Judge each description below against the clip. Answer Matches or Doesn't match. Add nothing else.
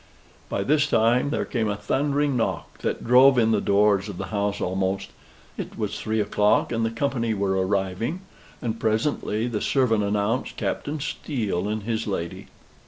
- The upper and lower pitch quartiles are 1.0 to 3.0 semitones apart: Doesn't match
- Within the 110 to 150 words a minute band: Doesn't match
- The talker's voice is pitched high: Doesn't match